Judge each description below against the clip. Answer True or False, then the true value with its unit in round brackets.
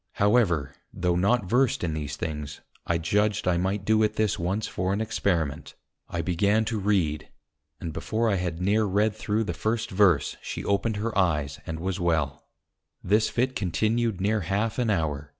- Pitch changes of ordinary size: True (4.4 semitones)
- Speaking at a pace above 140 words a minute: True (180 wpm)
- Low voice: True (100 Hz)